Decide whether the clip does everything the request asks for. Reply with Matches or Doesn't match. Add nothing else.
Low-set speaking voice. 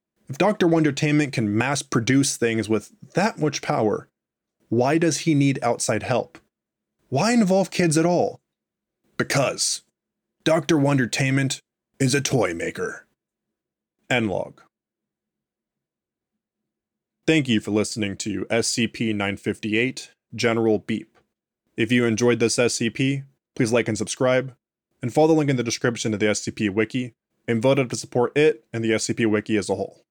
Matches